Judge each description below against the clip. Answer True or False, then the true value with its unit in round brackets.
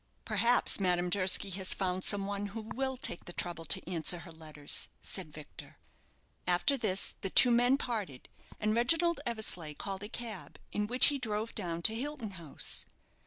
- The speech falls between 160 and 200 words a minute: True (170 wpm)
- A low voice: False (200 Hz)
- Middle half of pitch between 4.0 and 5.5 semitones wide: True (4.8 semitones)